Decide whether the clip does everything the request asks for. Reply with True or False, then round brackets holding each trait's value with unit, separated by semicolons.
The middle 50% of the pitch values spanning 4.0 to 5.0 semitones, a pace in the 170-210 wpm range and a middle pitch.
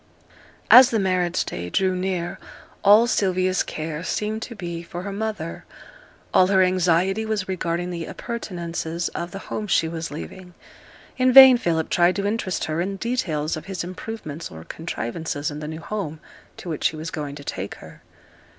False (3.6 semitones; 175 wpm; 180 Hz)